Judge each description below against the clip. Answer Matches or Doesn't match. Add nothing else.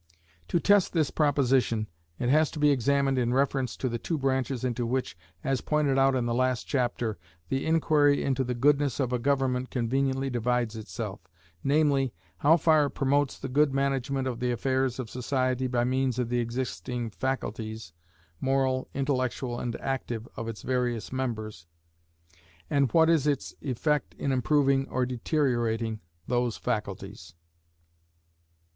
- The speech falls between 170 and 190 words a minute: Doesn't match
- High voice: Doesn't match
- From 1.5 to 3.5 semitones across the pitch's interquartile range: Matches